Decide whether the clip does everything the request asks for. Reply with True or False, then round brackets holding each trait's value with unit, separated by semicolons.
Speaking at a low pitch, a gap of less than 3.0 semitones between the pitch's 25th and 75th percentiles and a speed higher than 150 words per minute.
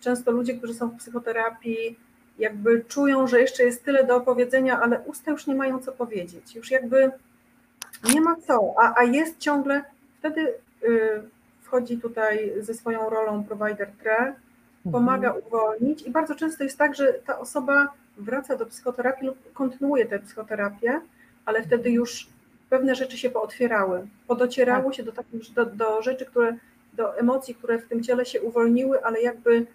False (245 Hz; 2.4 semitones; 160 wpm)